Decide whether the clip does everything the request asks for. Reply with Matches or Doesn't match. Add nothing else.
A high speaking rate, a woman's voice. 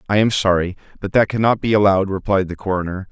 Doesn't match